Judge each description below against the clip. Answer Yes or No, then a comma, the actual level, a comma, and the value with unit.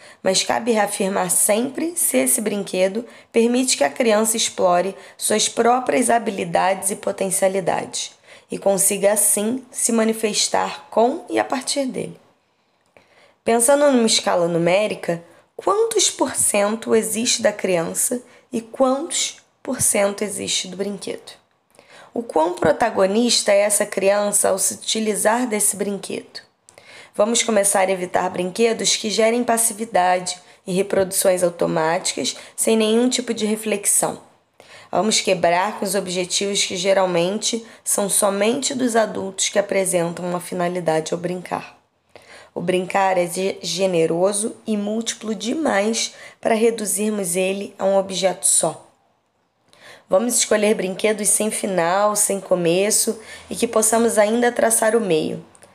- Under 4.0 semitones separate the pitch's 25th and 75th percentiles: Yes, average, 3.2 semitones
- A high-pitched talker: Yes, high, 210 Hz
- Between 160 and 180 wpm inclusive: No, average, 125 wpm